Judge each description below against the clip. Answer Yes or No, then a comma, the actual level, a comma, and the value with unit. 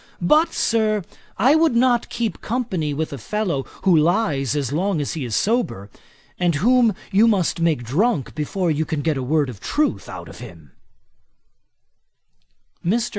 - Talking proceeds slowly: No, average, 165 wpm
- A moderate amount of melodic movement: No, wide, 7.6 semitones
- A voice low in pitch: No, medium, 175 Hz